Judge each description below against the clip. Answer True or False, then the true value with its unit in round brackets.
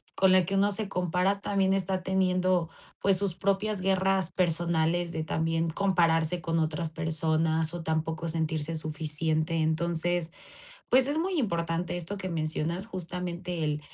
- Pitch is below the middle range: False (170 Hz)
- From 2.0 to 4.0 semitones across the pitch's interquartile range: True (2.8 semitones)